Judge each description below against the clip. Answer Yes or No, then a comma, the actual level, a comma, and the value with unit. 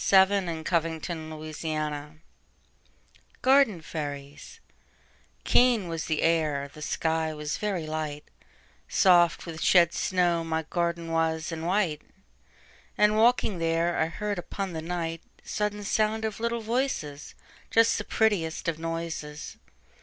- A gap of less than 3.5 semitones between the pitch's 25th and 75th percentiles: No, average, 3.9 semitones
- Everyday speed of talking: No, slow, 115 wpm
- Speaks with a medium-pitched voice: Yes, medium, 165 Hz